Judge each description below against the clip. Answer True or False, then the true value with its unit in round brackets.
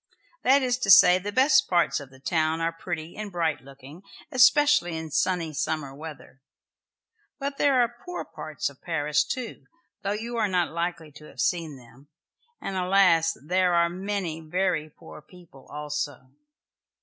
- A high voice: False (170 Hz)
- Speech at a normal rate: True (160 wpm)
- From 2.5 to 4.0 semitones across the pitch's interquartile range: False (4.6 semitones)